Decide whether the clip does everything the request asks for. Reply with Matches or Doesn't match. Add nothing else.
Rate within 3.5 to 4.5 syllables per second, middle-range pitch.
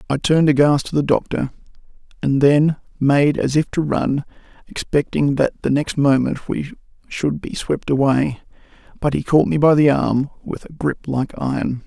Doesn't match